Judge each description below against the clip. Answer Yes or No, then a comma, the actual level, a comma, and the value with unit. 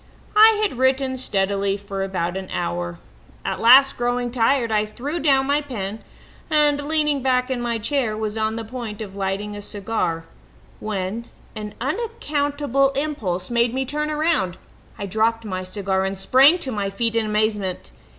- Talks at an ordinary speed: Yes, average, 165 wpm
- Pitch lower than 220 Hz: No, high, 230 Hz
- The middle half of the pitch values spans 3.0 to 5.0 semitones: No, wide, 5.4 semitones